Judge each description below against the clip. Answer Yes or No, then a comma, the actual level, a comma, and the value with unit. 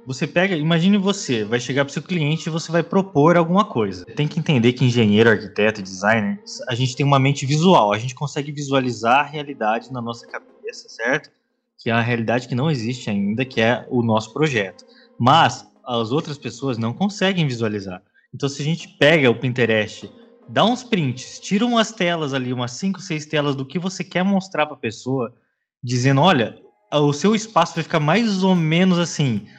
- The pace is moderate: No, fast, 195 wpm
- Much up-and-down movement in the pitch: Yes, wide, 6.4 semitones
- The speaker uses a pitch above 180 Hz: No, medium, 145 Hz